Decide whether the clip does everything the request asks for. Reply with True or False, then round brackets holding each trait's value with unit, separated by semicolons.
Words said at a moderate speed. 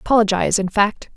True (155 wpm)